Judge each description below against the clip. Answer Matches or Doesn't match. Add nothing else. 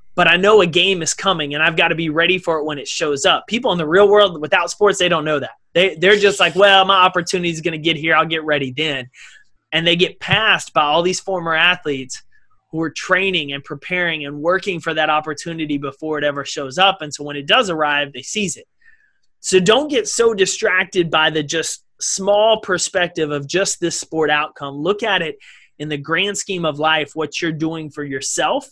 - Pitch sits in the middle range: Matches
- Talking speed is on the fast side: Matches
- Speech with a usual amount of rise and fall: Matches